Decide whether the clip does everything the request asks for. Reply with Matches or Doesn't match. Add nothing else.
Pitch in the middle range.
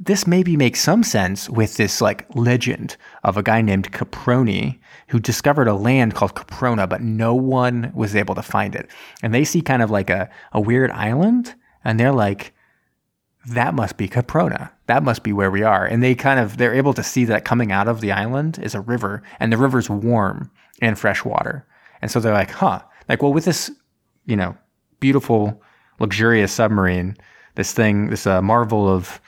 Doesn't match